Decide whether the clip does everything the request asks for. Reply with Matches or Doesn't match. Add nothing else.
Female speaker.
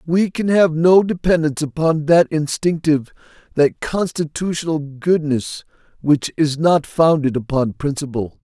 Doesn't match